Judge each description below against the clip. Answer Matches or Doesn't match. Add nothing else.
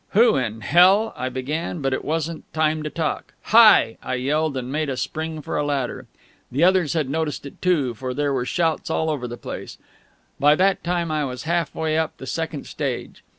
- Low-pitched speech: Doesn't match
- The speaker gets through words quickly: Matches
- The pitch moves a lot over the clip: Doesn't match